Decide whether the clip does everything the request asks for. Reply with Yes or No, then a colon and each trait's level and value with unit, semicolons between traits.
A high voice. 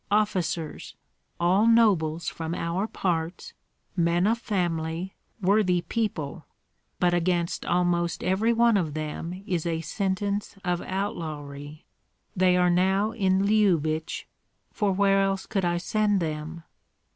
No: medium, 180 Hz